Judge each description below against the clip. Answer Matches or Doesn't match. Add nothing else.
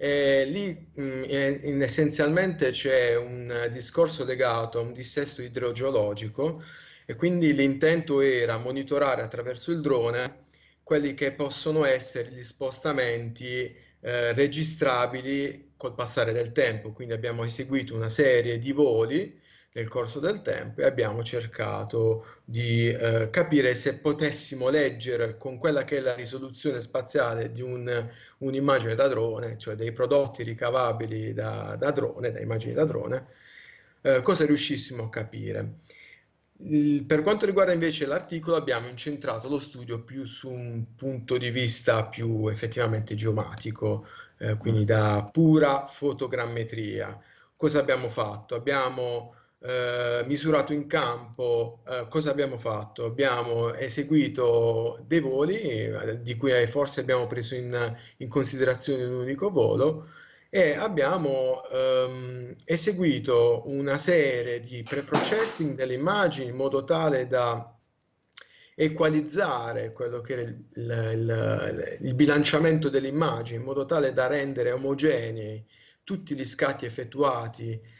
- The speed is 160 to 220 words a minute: Doesn't match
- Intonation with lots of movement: Doesn't match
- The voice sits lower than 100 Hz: Doesn't match